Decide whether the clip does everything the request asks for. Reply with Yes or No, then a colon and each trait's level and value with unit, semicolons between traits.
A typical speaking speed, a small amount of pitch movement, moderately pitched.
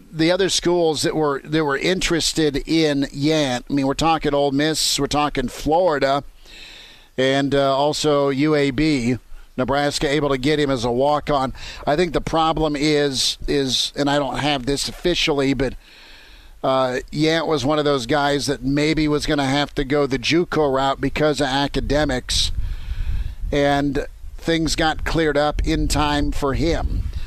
Yes: average, 165 wpm; narrow, 2.1 semitones; medium, 145 Hz